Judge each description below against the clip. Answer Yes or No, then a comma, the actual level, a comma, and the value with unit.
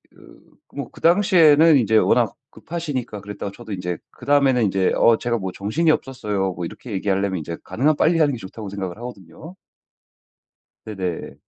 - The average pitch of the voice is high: No, low, 110 Hz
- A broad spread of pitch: Yes, wide, 7.0 semitones